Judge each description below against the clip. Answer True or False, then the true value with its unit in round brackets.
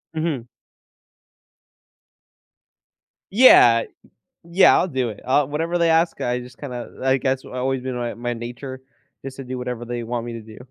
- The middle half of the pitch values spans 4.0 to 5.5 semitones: False (2.7 semitones)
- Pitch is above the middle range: False (130 Hz)